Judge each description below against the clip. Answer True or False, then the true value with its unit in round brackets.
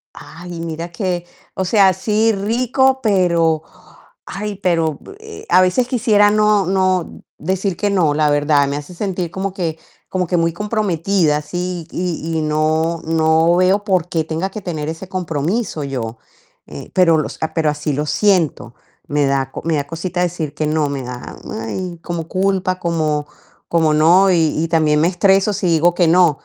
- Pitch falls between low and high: True (170 Hz)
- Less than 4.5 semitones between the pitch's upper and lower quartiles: True (3.5 semitones)